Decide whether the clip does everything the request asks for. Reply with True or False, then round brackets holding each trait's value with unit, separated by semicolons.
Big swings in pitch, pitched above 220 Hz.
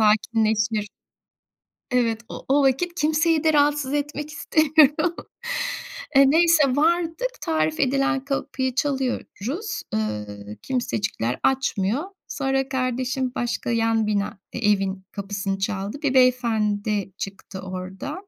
True (6.0 semitones; 250 Hz)